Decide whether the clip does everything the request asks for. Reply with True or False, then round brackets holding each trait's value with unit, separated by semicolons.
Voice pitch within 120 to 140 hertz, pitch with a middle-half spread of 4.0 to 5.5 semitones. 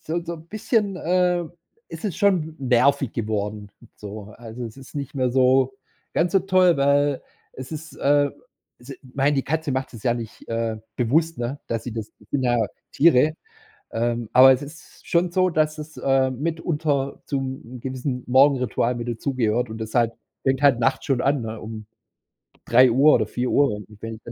True (135 Hz; 4.5 semitones)